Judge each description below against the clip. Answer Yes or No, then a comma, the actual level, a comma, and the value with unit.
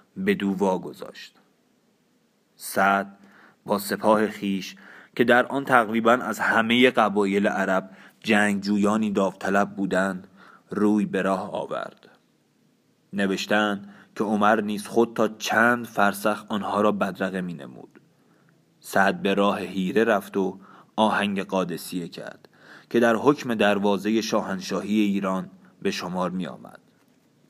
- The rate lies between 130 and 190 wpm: No, average, 120 wpm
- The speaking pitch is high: No, low, 105 Hz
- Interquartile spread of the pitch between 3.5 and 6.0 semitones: No, narrow, 2.6 semitones